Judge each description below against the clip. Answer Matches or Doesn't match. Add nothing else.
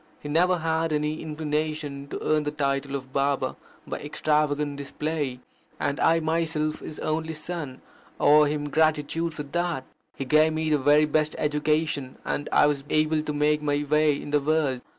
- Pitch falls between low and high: Matches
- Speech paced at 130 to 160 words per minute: Doesn't match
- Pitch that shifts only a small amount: Matches